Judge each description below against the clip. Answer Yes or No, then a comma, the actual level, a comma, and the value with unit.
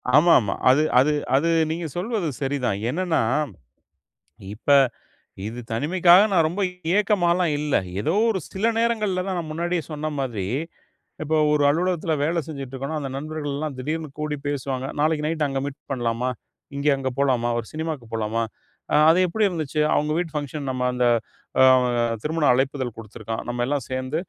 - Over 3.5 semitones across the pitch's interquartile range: Yes, average, 4.2 semitones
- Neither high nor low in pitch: Yes, medium, 150 Hz